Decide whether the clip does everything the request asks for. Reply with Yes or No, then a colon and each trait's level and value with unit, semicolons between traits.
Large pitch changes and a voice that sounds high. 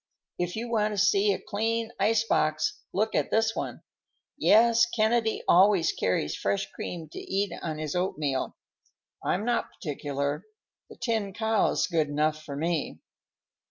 Yes: wide, 6.2 semitones; high, 195 Hz